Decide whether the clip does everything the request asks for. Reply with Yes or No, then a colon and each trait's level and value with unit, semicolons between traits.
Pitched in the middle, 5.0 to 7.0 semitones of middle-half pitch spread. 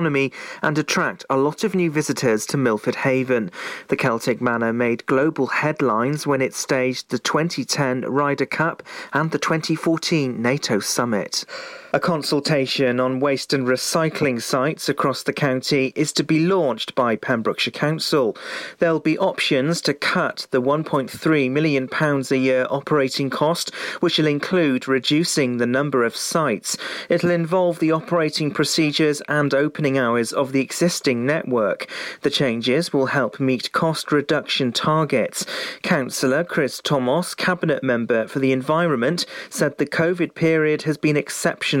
No: medium, 145 Hz; average, 3.3 semitones